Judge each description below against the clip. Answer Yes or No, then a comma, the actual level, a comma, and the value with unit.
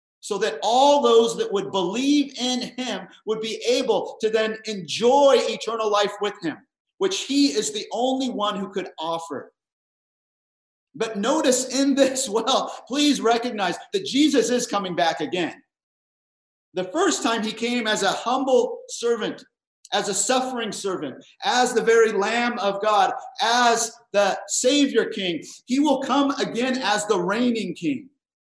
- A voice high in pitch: Yes, high, 235 Hz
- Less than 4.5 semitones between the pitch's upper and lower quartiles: No, average, 4.9 semitones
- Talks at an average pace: Yes, average, 150 wpm